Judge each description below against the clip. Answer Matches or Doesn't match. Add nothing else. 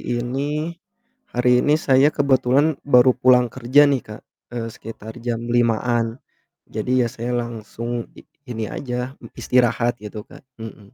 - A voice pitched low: Matches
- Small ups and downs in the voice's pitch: Matches